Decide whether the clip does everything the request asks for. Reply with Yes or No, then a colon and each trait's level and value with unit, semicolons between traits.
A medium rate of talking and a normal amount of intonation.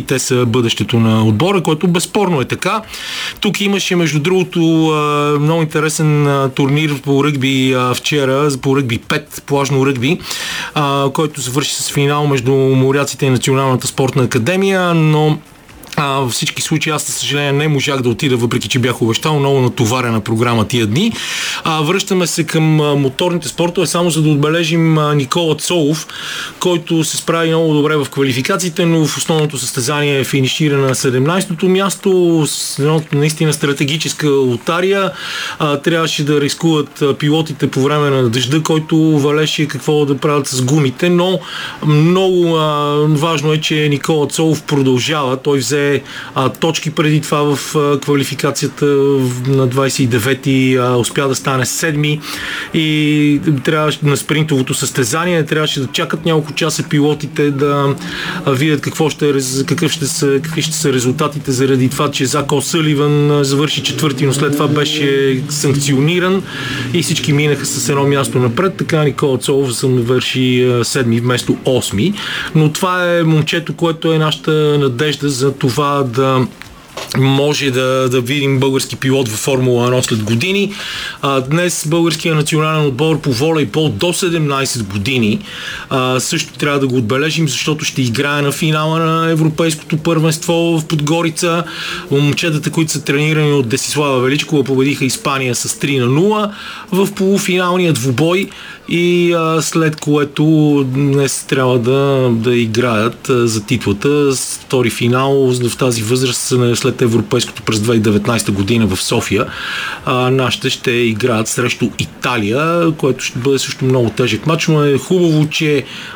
Yes: average, 145 wpm; average, 3.2 semitones